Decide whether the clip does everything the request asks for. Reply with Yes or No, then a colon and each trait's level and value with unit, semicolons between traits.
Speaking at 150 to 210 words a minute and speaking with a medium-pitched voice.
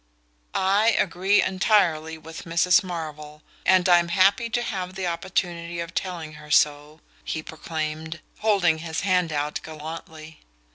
No: slow, 135 wpm; medium, 170 Hz